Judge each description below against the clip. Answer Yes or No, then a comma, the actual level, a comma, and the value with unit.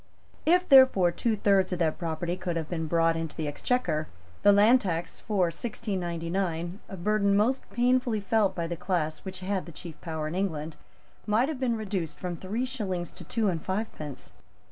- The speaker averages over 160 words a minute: Yes, average, 185 wpm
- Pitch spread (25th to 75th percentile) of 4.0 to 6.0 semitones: Yes, average, 4.3 semitones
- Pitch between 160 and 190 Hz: Yes, medium, 185 Hz